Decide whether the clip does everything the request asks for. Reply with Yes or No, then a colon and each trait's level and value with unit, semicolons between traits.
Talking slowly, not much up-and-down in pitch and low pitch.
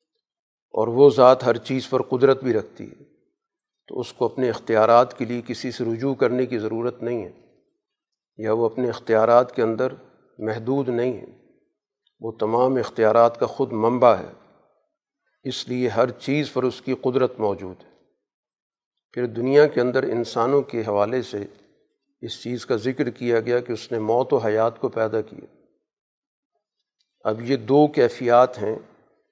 No: average, 160 wpm; narrow, 2.1 semitones; low, 120 Hz